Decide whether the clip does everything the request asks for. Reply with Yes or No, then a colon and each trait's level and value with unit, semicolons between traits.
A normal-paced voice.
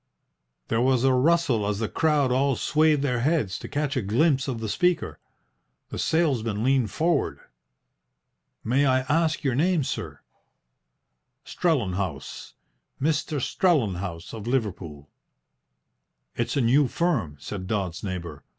No: slow, 130 wpm